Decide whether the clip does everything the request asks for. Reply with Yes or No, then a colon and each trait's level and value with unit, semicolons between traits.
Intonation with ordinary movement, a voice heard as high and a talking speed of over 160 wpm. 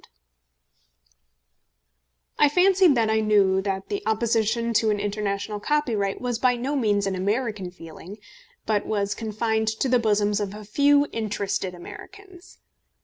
No: average, 3.5 semitones; high, 215 Hz; average, 145 wpm